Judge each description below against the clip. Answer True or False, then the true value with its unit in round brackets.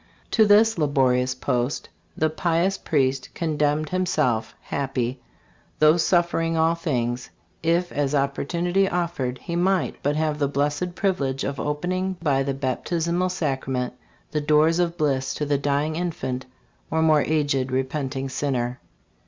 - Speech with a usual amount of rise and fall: True (4.0 semitones)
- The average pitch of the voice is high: False (150 Hz)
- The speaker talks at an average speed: True (145 wpm)